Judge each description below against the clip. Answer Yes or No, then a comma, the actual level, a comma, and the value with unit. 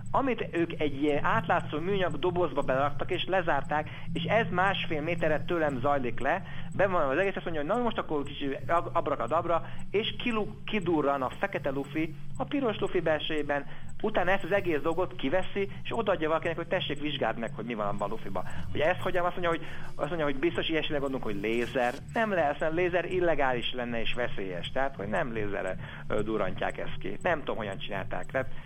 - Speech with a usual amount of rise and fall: Yes, average, 4.0 semitones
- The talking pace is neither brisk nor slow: No, fast, 190 wpm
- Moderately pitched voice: Yes, medium, 160 Hz